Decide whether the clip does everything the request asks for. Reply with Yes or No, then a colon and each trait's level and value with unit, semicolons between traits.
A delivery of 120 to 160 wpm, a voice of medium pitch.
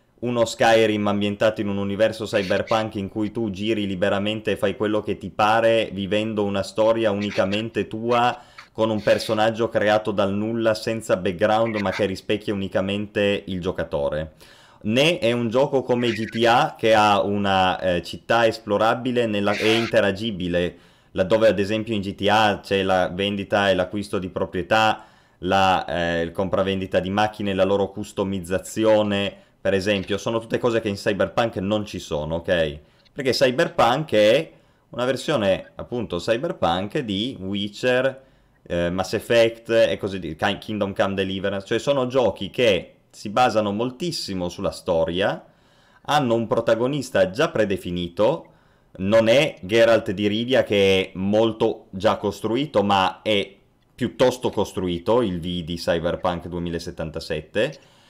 No: average, 140 wpm; low, 105 Hz